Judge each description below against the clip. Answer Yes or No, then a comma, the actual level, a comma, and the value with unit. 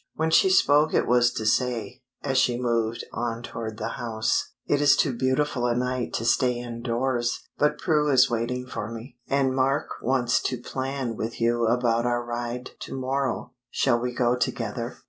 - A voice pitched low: Yes, low, 125 Hz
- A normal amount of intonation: No, narrow, 2.0 semitones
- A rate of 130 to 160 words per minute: No, average, 185 wpm